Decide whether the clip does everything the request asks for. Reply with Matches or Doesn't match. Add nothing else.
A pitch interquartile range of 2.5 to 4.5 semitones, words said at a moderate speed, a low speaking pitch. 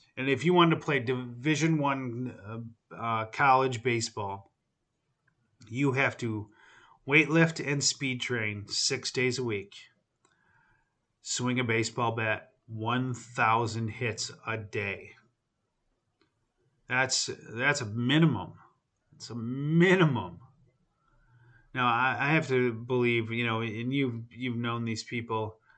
Doesn't match